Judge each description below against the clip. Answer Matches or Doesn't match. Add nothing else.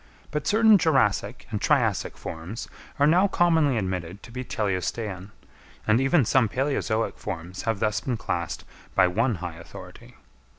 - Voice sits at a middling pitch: Doesn't match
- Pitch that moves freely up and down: Matches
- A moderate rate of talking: Matches